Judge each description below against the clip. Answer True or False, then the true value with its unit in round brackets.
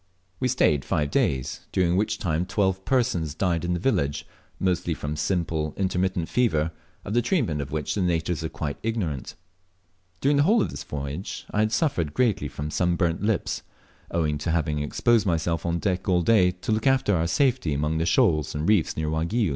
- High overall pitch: False (85 Hz)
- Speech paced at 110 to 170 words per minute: False (190 wpm)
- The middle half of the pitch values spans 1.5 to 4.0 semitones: False (5.3 semitones)